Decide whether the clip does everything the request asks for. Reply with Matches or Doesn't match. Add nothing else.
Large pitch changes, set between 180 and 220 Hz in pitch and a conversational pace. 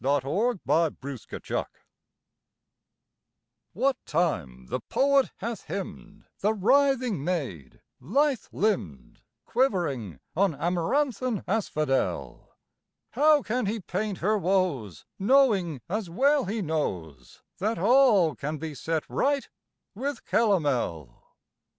Doesn't match